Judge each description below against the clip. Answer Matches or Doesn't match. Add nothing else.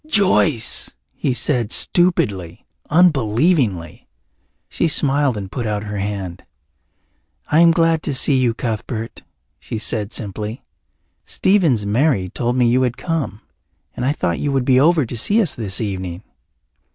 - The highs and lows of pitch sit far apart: Matches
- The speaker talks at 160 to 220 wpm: Doesn't match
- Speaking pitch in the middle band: Doesn't match